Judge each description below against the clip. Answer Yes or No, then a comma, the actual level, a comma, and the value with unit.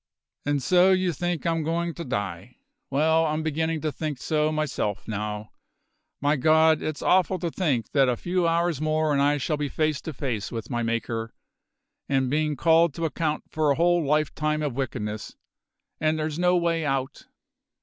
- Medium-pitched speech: Yes, medium, 155 Hz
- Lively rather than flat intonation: No, average, 3.4 semitones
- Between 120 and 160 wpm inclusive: No, average, 180 wpm